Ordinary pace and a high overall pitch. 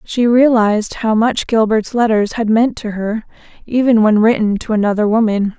Yes: average, 170 wpm; high, 220 Hz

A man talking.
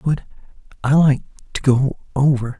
Yes: male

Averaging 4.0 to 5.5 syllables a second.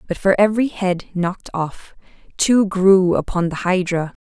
Yes: 4.6 syllables/s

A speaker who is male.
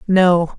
No: female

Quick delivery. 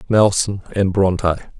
No: slow, 115 wpm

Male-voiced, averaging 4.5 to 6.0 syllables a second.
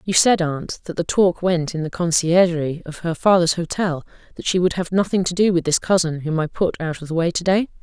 No: female; 5.5 syllables/s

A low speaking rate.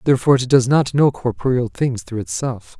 No: average, 195 wpm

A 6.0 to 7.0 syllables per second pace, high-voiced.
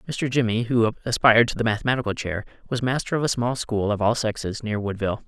No: 6.4 syllables/s; low, 115 Hz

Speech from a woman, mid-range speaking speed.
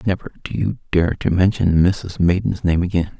No: male; average, 190 wpm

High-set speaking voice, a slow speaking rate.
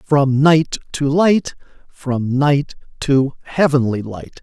No: medium, 140 Hz; slow, 120 wpm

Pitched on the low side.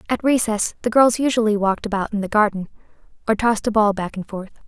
No: high, 215 Hz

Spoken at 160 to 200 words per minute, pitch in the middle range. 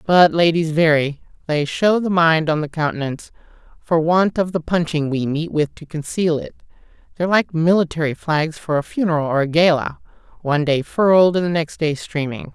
Yes: average, 180 wpm; medium, 160 Hz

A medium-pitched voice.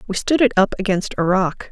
No: high, 200 Hz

